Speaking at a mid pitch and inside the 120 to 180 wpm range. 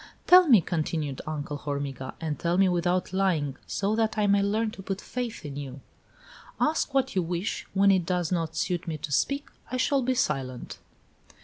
No: medium, 180 Hz; average, 195 wpm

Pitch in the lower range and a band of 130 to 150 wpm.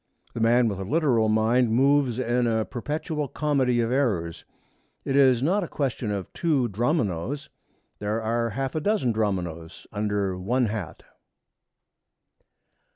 Yes: low, 120 Hz; average, 140 wpm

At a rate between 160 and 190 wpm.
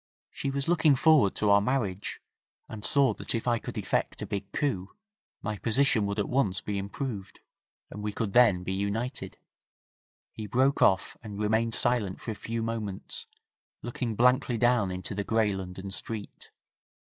Yes: average, 170 wpm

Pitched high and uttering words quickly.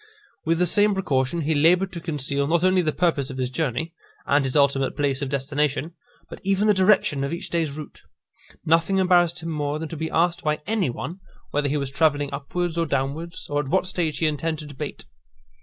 No: medium, 155 Hz; fast, 210 wpm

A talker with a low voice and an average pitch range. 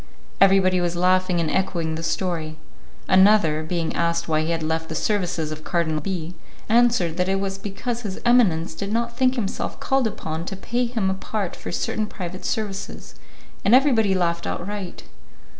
No: medium, 185 Hz; average, 3.9 semitones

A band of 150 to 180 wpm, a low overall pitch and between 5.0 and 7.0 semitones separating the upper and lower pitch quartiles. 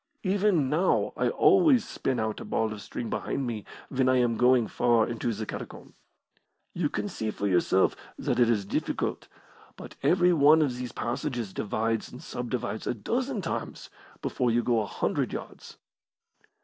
Yes: average, 170 wpm; low, 125 Hz; wide, 5.5 semitones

